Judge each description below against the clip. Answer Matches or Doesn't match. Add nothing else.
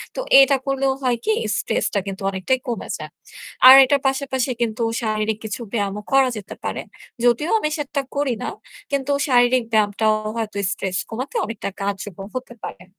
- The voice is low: Doesn't match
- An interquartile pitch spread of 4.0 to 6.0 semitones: Matches